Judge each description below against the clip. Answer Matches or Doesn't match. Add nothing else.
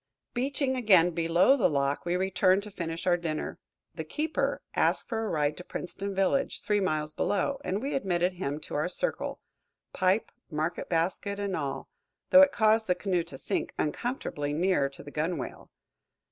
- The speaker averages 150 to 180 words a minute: Matches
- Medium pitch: Matches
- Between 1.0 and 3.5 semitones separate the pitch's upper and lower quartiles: Doesn't match